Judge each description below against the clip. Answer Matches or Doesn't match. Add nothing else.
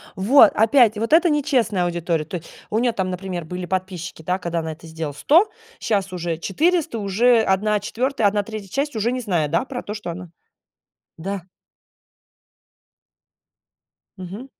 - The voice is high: Matches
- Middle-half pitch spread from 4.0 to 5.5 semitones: Matches